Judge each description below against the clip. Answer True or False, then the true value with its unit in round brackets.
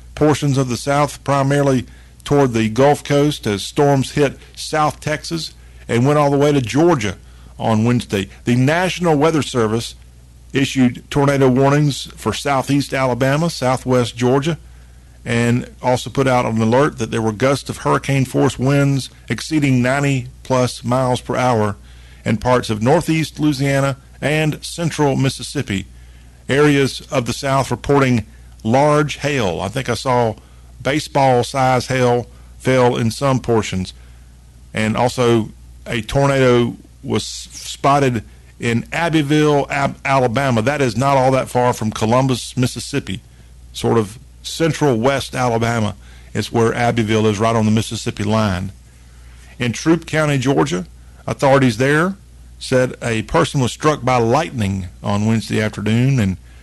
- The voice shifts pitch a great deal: False (4.4 semitones)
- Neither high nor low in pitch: False (125 Hz)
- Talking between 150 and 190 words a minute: False (140 wpm)